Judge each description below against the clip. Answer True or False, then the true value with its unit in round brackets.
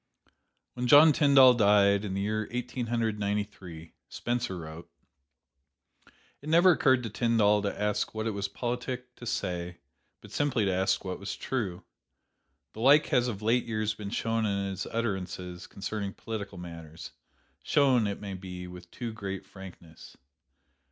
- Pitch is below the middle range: True (105 Hz)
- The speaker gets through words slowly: False (160 wpm)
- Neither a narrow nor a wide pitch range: True (4.0 semitones)